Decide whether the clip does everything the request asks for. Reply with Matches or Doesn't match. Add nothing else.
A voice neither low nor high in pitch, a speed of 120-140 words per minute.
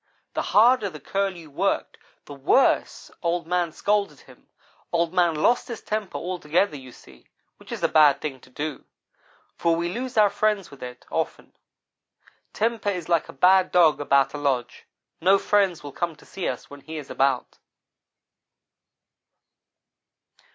Doesn't match